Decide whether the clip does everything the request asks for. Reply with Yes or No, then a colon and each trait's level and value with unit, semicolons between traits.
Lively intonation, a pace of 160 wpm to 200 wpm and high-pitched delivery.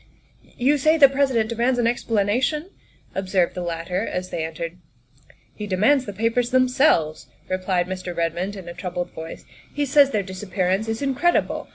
Yes: wide, 6.1 semitones; average, 175 wpm; high, 205 Hz